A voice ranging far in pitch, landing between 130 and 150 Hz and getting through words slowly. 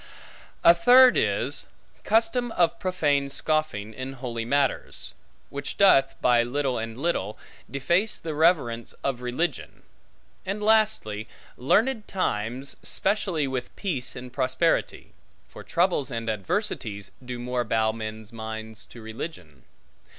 Yes: wide, 7.1 semitones; low, 135 Hz; slow, 120 wpm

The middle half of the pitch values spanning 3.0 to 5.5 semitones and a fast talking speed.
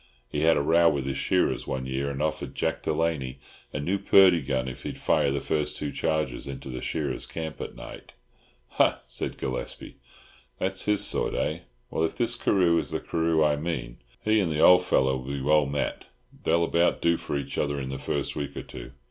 Yes: average, 3.7 semitones; fast, 210 wpm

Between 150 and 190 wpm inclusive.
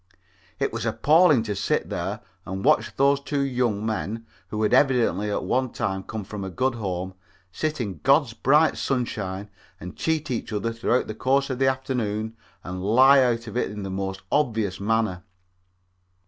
Yes: average, 175 wpm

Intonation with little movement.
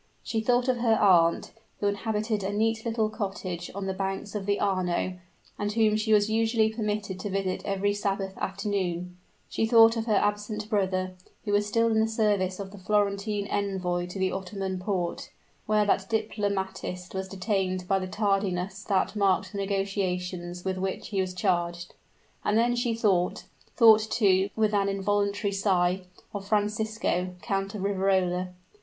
Yes: narrow, 2.2 semitones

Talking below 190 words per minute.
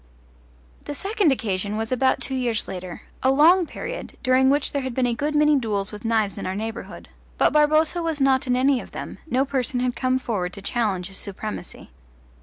No: fast, 205 wpm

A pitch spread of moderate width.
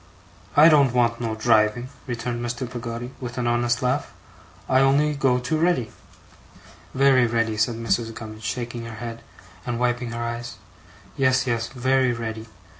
No: narrow, 1.9 semitones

